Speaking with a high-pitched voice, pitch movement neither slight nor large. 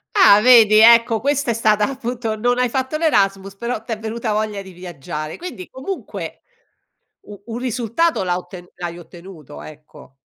Yes: high, 220 Hz; average, 4.5 semitones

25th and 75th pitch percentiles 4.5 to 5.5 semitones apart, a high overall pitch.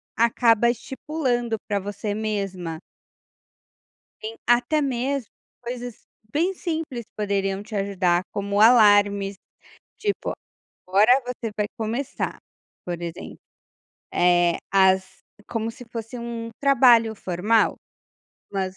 No: average, 3.6 semitones; high, 220 Hz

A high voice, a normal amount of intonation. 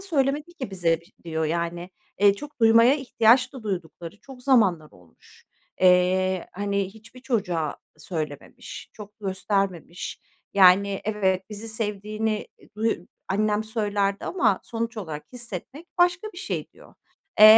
Yes: high, 205 Hz; average, 4.1 semitones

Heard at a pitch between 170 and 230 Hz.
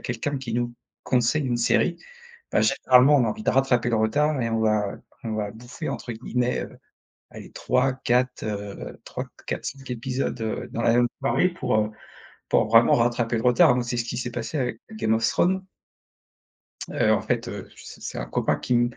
No: low, 120 Hz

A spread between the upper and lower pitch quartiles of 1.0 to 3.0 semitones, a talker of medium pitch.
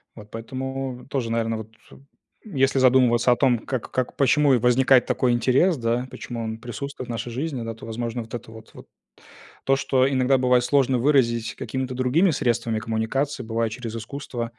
No: narrow, 2.5 semitones; low, 125 Hz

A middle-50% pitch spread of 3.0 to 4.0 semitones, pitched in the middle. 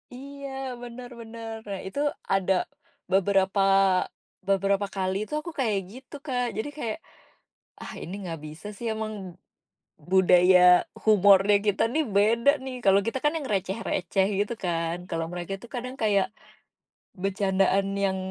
No: average, 3.6 semitones; high, 200 Hz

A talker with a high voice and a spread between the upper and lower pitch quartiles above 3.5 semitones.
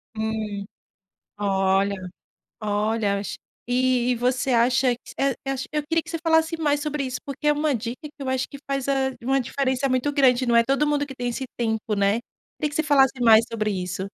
Yes: very high, 255 Hz; average, 4.2 semitones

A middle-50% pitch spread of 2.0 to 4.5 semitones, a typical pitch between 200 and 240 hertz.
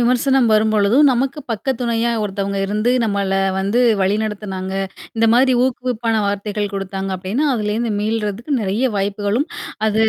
Yes: average, 2.9 semitones; high, 215 Hz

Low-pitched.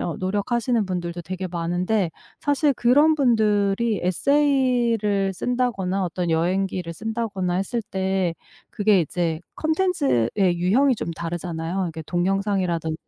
No: high, 195 Hz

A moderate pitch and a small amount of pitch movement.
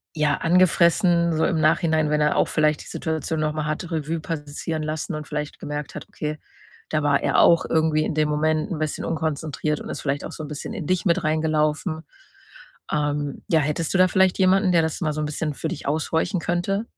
Yes: medium, 155 Hz; narrow, 1.7 semitones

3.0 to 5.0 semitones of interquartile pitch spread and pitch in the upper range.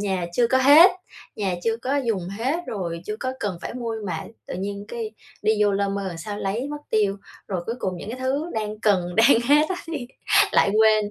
Yes: average, 4.3 semitones; high, 215 Hz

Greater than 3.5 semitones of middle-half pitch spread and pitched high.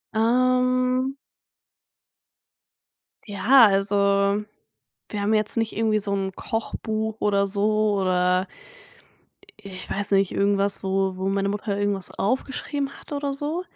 Yes: average, 4.2 semitones; high, 210 Hz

